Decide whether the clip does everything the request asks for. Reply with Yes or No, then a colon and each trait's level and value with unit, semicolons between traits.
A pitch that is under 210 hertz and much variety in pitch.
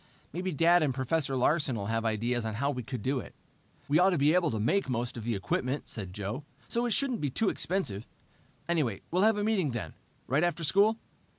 Yes: medium, 140 Hz; wide, 7.1 semitones